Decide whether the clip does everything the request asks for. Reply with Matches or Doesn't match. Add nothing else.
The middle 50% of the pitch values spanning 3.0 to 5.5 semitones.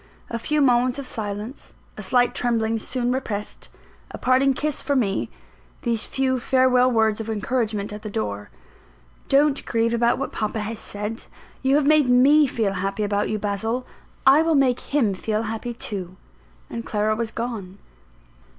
Matches